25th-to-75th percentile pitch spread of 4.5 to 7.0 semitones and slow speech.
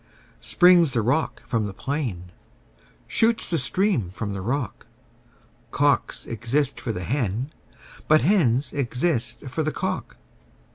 Yes: wide, 5.5 semitones; slow, 130 wpm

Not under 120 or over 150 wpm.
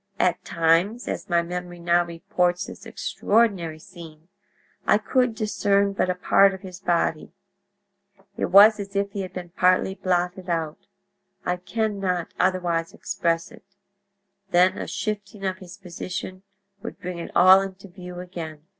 Yes: average, 145 wpm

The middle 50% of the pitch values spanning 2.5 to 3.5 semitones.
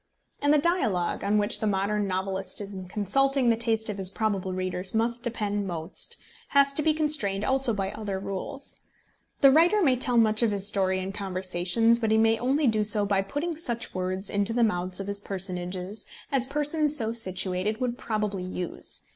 No: average, 4.1 semitones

